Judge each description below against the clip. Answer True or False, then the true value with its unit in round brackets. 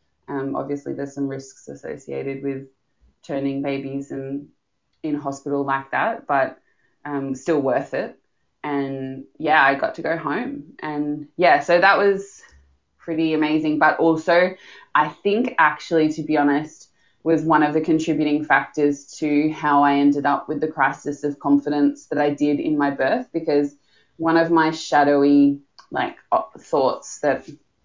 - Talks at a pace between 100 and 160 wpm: True (155 wpm)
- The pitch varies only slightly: True (1.9 semitones)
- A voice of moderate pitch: True (145 Hz)